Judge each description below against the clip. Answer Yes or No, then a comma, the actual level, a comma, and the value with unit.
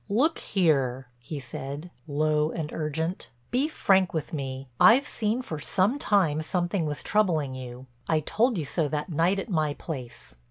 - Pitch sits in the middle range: Yes, medium, 155 Hz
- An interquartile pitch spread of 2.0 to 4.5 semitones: No, average, 5.3 semitones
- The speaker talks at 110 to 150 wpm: No, average, 160 wpm